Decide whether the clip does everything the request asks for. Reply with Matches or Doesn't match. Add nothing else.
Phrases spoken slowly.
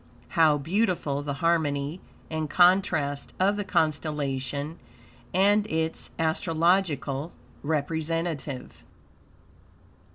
Matches